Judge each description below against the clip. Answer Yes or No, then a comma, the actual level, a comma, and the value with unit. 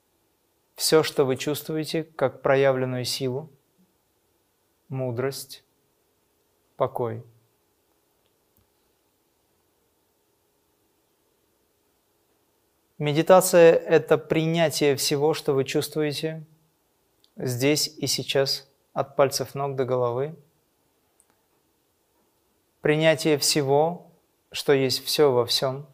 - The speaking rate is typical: No, slow, 70 wpm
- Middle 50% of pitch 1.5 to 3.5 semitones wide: Yes, average, 2.8 semitones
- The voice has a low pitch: No, medium, 145 Hz